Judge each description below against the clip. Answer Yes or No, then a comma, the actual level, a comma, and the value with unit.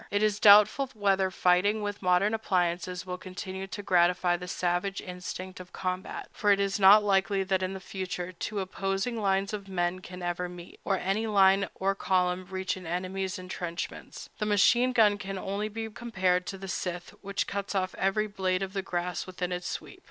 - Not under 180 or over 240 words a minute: Yes, average, 190 wpm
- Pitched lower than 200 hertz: Yes, high, 190 Hz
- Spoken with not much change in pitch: Yes, narrow, 1.8 semitones